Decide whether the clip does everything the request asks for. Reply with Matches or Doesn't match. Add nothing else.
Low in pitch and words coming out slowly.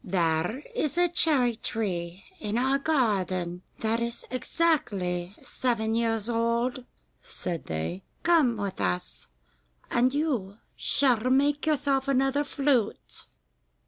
Doesn't match